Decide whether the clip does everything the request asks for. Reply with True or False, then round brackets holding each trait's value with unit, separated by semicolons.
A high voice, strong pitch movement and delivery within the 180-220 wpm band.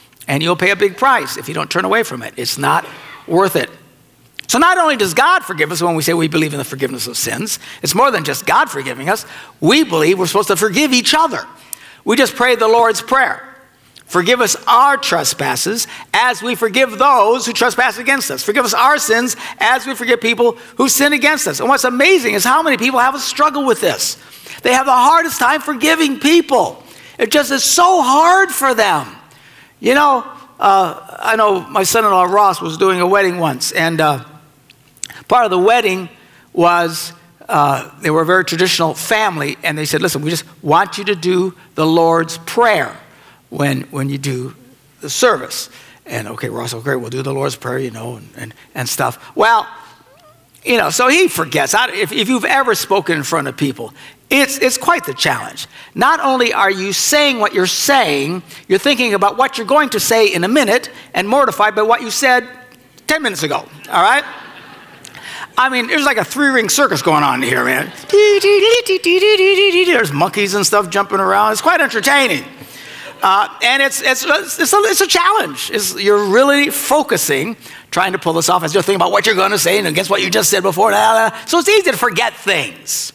True (225 Hz; 8.6 semitones; 205 wpm)